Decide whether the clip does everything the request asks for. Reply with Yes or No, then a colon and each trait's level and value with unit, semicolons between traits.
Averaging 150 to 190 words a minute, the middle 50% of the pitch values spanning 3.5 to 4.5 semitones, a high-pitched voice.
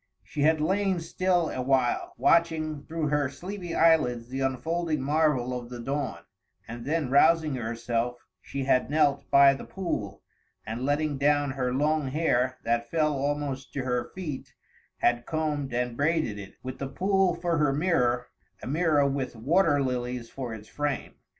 No: average, 165 wpm; average, 4.1 semitones; medium, 140 Hz